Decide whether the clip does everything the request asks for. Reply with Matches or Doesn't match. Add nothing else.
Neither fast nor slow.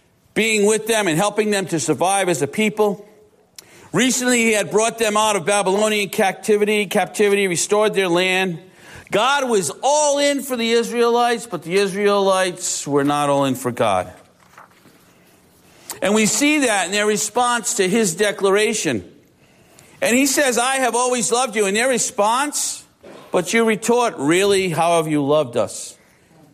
Matches